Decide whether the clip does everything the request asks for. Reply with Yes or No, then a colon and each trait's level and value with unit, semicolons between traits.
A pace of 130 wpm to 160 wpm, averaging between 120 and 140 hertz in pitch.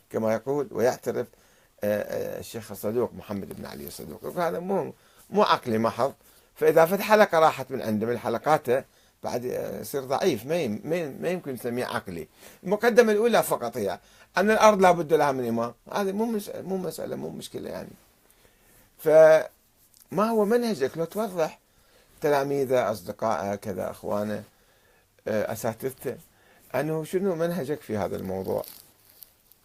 No: fast, 135 wpm; medium, 150 Hz